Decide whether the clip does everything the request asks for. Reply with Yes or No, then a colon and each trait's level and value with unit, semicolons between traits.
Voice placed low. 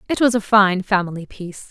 No: high, 200 Hz